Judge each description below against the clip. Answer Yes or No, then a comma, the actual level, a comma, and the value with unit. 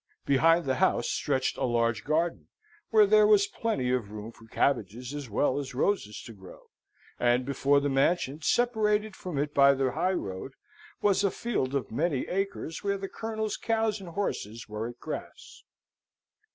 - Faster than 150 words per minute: Yes, average, 165 wpm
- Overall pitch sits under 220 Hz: Yes, medium, 140 Hz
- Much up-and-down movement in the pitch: Yes, wide, 8.1 semitones